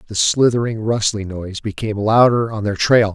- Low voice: Yes, low, 105 Hz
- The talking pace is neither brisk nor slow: Yes, average, 170 wpm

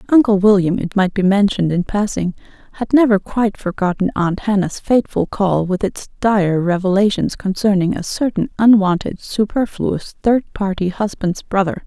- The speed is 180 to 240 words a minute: No, average, 140 wpm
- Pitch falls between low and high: No, high, 200 Hz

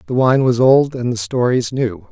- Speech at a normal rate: No, fast, 225 wpm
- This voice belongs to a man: Yes, male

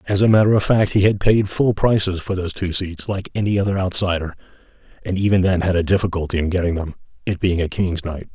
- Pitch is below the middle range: Yes, very low, 95 Hz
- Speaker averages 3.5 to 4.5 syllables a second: No, 6.2 syllables/s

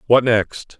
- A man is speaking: Yes, male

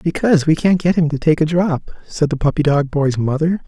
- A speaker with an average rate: No, fast, 245 wpm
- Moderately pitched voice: Yes, medium, 155 Hz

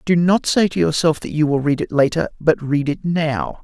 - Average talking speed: No, fast, 245 wpm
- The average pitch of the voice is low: No, medium, 150 Hz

